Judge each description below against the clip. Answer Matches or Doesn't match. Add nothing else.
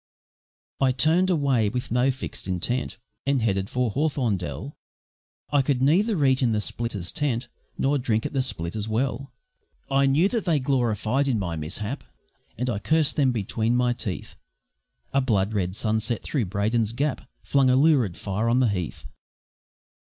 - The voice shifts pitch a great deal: Doesn't match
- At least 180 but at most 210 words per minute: Doesn't match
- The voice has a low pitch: Matches